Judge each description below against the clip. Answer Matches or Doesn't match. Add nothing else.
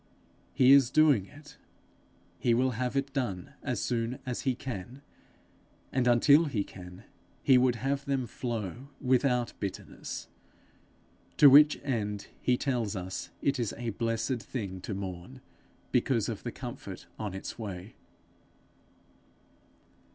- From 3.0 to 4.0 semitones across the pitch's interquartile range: Doesn't match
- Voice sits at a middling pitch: Doesn't match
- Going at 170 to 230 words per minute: Doesn't match